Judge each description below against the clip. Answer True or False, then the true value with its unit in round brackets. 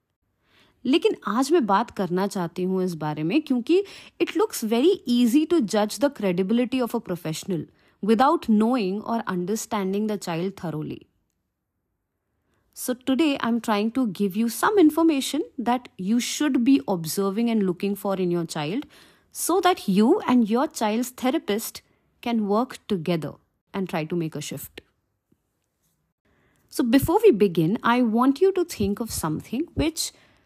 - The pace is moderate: True (155 wpm)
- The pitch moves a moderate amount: False (6.5 semitones)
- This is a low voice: False (220 Hz)